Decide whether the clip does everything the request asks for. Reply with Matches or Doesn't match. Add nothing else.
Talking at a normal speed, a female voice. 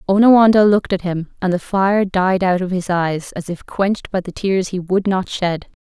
Doesn't match